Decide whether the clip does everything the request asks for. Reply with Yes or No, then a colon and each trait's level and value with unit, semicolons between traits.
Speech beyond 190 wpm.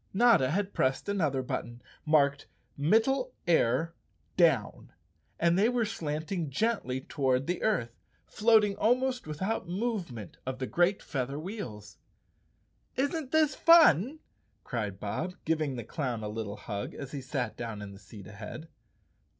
No: average, 140 wpm